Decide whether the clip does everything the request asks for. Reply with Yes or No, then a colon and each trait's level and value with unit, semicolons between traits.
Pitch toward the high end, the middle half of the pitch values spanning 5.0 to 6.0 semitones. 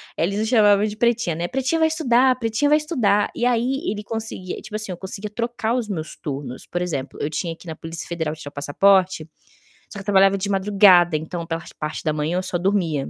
Yes: high, 195 Hz; average, 5.3 semitones